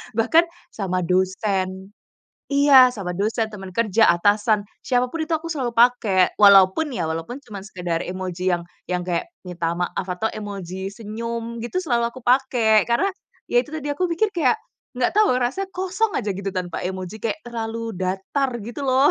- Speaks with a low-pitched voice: No, high, 225 Hz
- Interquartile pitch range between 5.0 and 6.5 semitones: Yes, wide, 5.5 semitones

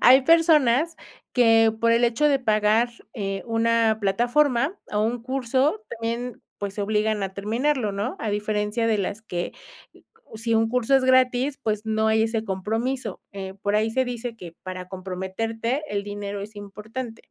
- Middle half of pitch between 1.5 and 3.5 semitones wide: Yes, average, 3.1 semitones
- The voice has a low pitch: No, high, 225 Hz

